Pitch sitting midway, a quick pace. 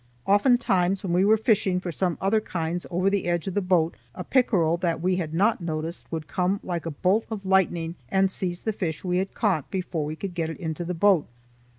Yes: medium, 180 Hz; fast, 225 wpm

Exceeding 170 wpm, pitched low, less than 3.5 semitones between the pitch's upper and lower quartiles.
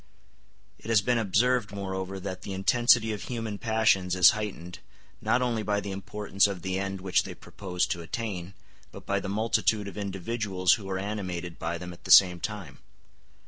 Yes: average, 185 wpm; low, 100 Hz; average, 2.7 semitones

